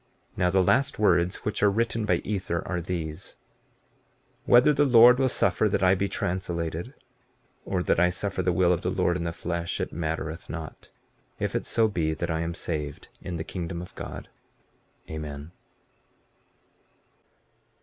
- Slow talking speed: No, average, 165 wpm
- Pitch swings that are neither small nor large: Yes, average, 3.2 semitones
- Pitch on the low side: Yes, very low, 90 Hz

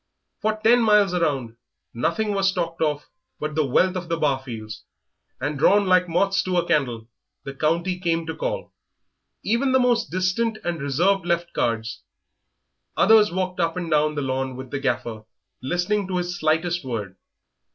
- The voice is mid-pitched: Yes, medium, 170 Hz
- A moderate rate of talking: Yes, average, 165 wpm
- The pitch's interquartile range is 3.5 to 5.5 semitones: Yes, average, 5.2 semitones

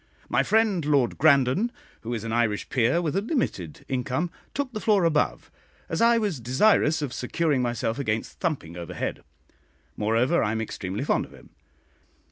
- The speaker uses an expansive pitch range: Yes, wide, 7.4 semitones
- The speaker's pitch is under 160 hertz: Yes, low, 135 Hz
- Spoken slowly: No, average, 165 wpm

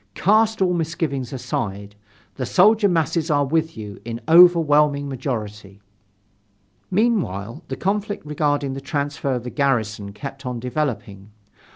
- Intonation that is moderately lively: No, wide, 6.0 semitones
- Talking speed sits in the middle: No, slow, 130 wpm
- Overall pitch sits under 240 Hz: Yes, medium, 140 Hz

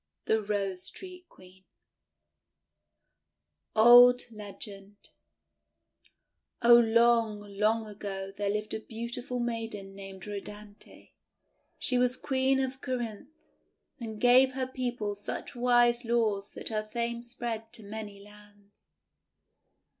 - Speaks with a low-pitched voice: No, high, 225 Hz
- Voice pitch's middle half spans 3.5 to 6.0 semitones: No, average, 2.9 semitones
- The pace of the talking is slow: Yes, slow, 110 wpm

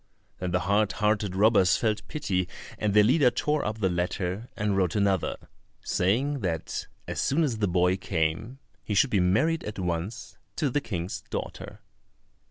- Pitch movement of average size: Yes, average, 3.8 semitones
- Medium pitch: No, low, 100 Hz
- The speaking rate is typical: Yes, average, 170 wpm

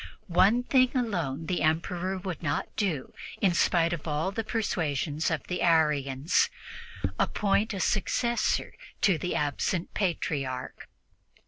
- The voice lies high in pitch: No, medium, 175 Hz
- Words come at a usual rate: No, slow, 125 wpm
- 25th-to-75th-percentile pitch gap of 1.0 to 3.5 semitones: No, average, 4.5 semitones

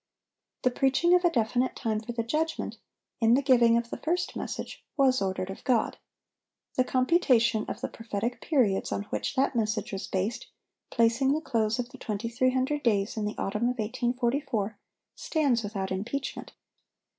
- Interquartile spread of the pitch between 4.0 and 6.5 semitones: No, average, 3.5 semitones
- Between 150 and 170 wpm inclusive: Yes, average, 165 wpm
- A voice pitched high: Yes, high, 235 Hz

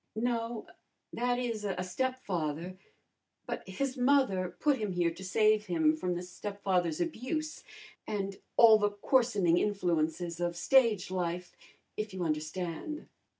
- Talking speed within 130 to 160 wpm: Yes, slow, 135 wpm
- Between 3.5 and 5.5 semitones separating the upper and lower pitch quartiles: Yes, average, 4.9 semitones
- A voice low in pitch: No, high, 195 Hz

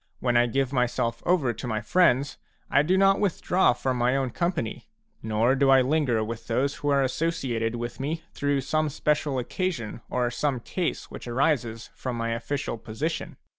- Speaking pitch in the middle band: No, low, 130 Hz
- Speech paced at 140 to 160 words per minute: No, average, 170 wpm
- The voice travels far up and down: No, average, 4.0 semitones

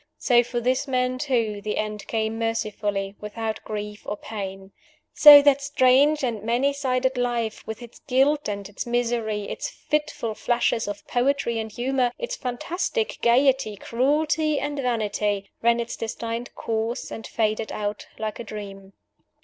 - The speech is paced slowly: No, average, 150 wpm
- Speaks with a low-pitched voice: No, high, 235 Hz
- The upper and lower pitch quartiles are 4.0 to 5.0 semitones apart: No, average, 3.5 semitones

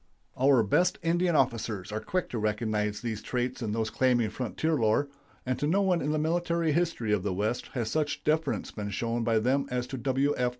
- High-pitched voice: No, low, 125 Hz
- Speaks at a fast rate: Yes, fast, 210 wpm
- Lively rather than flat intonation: Yes, wide, 5.8 semitones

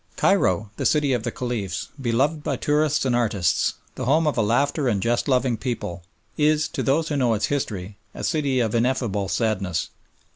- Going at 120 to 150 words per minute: No, average, 185 wpm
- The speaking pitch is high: No, low, 125 Hz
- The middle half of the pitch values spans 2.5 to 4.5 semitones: No, average, 5.1 semitones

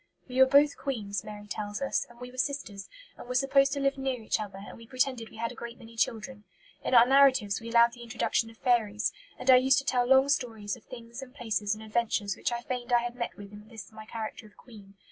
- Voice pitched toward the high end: Yes, high, 235 Hz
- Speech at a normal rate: No, fast, 250 wpm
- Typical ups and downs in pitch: Yes, average, 3.2 semitones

